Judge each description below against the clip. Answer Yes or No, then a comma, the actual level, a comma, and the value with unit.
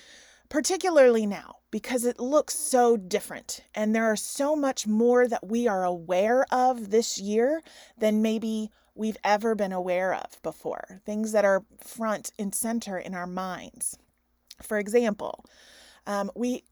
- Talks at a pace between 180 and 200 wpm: No, average, 145 wpm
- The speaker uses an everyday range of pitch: Yes, average, 3.6 semitones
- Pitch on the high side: Yes, high, 225 Hz